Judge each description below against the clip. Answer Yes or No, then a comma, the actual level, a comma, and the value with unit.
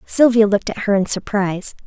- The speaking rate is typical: Yes, average, 195 wpm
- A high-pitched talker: Yes, high, 205 Hz